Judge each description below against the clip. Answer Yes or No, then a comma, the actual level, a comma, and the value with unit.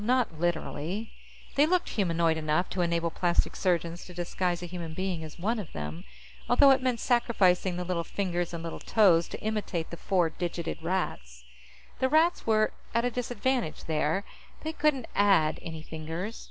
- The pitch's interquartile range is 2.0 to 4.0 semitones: No, average, 5.1 semitones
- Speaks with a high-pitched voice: No, medium, 180 Hz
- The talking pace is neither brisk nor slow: Yes, average, 170 wpm